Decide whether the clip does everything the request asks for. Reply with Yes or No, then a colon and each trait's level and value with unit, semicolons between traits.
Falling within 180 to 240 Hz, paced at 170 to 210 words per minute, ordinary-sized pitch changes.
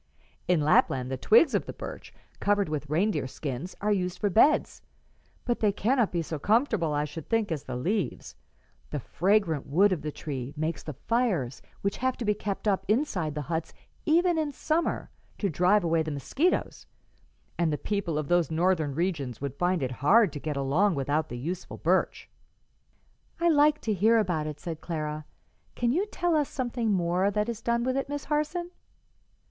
No: medium, 185 Hz; average, 185 wpm; wide, 7.1 semitones